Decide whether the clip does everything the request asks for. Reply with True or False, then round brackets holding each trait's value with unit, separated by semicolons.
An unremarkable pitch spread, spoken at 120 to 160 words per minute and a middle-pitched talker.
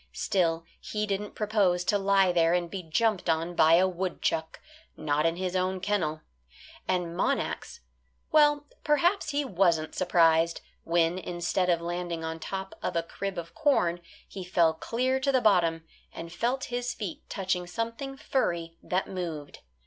True (3.7 semitones; 155 wpm; 180 Hz)